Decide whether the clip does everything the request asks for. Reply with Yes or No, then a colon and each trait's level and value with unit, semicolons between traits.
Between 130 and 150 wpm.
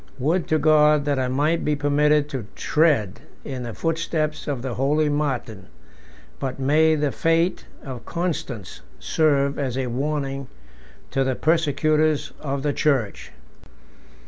Yes: average, 140 wpm